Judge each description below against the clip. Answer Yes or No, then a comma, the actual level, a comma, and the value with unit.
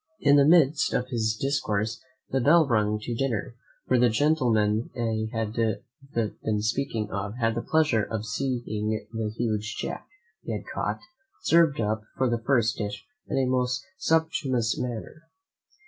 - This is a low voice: Yes, low, 115 Hz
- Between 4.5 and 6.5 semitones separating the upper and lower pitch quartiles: No, average, 3.8 semitones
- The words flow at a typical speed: Yes, average, 155 wpm